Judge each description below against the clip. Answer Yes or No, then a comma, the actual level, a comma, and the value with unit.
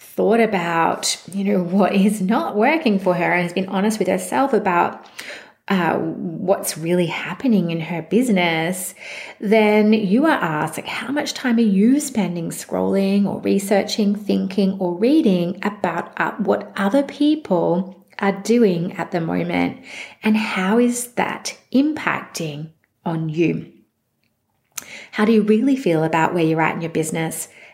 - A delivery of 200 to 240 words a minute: No, average, 150 wpm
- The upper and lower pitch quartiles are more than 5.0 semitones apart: No, average, 4.2 semitones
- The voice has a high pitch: Yes, high, 195 Hz